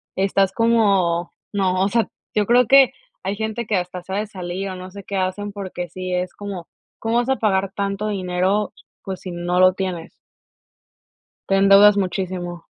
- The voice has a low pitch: No, high, 195 Hz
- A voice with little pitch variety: Yes, narrow, 2.1 semitones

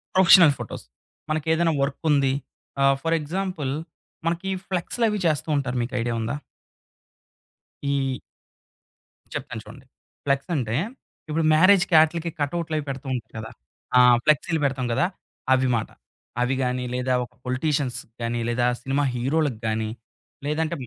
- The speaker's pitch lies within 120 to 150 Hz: Yes, medium, 140 Hz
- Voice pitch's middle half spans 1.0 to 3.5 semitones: No, average, 4.3 semitones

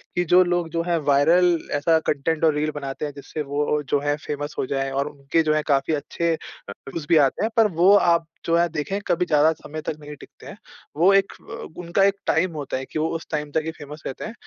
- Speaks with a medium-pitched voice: Yes, medium, 155 Hz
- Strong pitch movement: No, narrow, 2.6 semitones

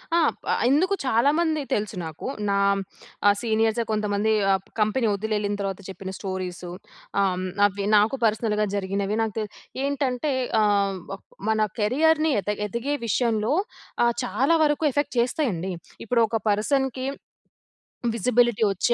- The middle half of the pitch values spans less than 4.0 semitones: No, average, 4.3 semitones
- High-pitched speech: Yes, high, 220 Hz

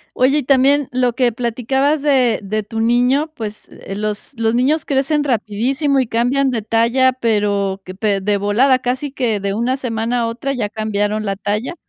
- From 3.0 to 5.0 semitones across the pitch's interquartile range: Yes, average, 3.9 semitones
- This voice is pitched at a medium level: No, high, 235 Hz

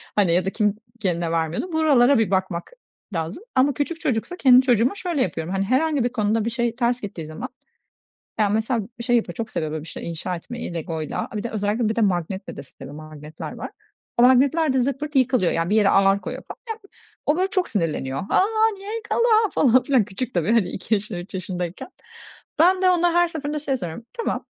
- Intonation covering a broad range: Yes, wide, 7.0 semitones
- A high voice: Yes, high, 225 Hz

